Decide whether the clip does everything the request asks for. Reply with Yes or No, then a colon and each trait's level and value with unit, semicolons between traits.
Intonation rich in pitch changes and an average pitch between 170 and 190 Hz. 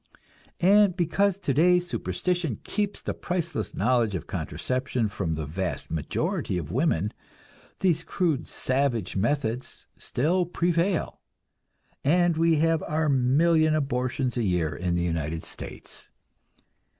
No: wide, 8.3 semitones; medium, 140 Hz